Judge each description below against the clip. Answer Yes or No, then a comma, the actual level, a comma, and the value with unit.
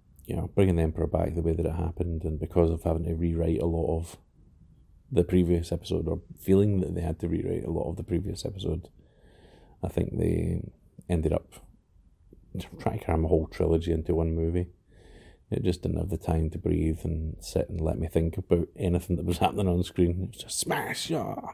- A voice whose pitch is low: Yes, very low, 85 Hz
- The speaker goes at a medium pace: No, fast, 210 wpm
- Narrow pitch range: Yes, narrow, 1.8 semitones